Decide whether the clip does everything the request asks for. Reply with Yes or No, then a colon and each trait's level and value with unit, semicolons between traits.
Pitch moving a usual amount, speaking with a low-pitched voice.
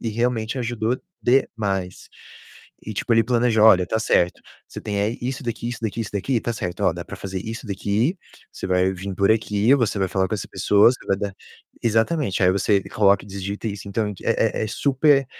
Yes: average, 3.1 semitones; low, 110 Hz